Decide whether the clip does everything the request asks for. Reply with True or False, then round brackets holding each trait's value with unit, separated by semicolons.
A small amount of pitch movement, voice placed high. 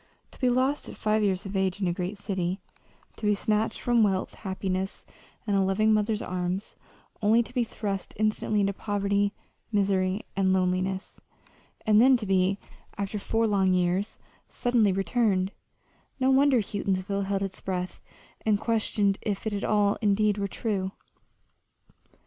True (2.1 semitones; 200 Hz)